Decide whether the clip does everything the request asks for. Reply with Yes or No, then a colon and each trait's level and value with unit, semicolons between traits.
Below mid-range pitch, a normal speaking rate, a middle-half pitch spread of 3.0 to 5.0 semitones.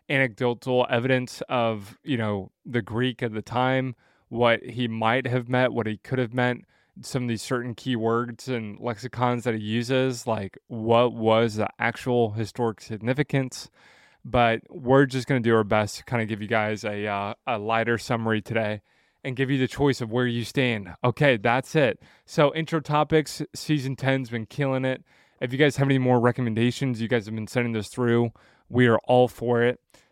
No: low, 120 Hz; average, 190 wpm; narrow, 2.4 semitones